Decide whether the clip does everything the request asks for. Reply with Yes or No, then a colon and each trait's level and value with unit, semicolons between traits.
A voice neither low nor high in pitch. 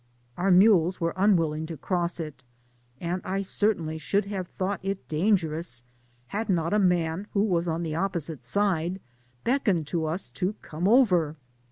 Yes: medium, 180 Hz